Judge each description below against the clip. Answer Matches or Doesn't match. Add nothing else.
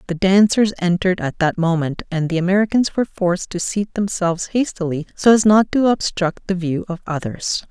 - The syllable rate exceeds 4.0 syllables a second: Matches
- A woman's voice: Matches